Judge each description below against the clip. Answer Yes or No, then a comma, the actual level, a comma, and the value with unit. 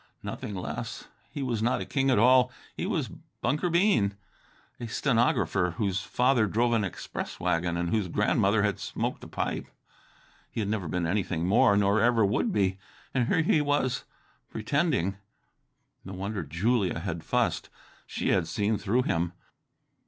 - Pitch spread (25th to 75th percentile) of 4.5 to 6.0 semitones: Yes, average, 5.1 semitones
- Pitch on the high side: No, low, 105 Hz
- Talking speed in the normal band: Yes, average, 160 wpm